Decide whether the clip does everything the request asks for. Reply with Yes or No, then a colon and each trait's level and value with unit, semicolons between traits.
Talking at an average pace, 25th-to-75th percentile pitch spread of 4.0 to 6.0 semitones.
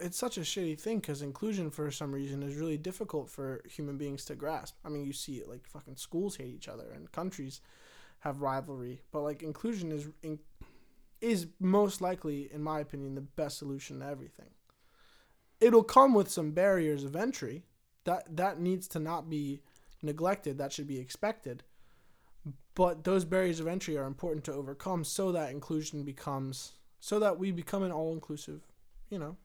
Yes: average, 180 wpm; average, 4.5 semitones